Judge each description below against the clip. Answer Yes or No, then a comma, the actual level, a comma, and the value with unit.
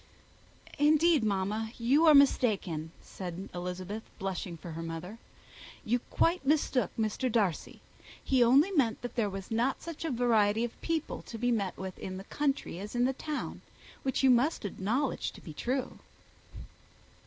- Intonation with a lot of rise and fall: Yes, wide, 5.9 semitones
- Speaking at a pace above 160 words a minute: No, average, 155 wpm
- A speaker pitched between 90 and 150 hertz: No, high, 230 Hz